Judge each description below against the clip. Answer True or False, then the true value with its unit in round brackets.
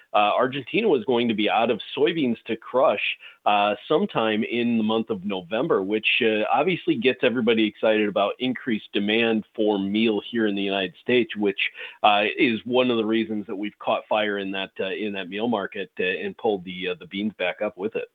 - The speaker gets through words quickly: True (210 wpm)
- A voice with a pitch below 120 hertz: True (110 Hz)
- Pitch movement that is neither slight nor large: False (2.0 semitones)